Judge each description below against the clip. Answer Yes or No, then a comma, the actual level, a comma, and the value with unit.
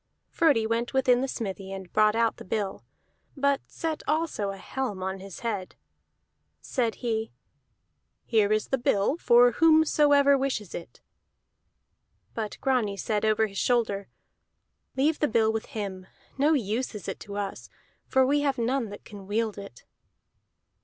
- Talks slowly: No, average, 155 wpm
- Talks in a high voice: Yes, high, 225 Hz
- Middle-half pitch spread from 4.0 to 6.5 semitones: Yes, average, 4.7 semitones